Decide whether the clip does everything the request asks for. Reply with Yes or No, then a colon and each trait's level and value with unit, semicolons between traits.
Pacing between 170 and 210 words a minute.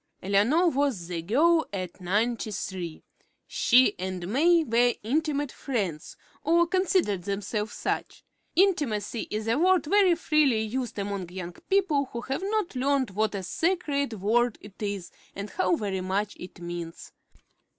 No: average, 145 wpm